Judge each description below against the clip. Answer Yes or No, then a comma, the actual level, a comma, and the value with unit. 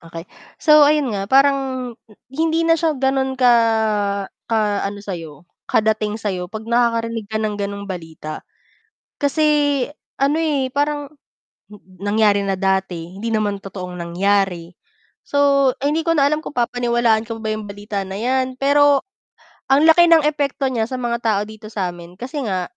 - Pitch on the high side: Yes, high, 230 Hz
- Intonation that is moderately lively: No, wide, 5.9 semitones